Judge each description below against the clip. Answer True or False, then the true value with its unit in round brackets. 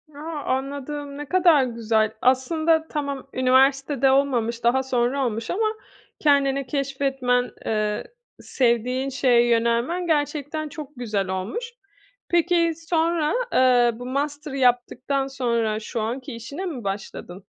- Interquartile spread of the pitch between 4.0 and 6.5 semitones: False (3.5 semitones)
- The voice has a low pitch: False (265 Hz)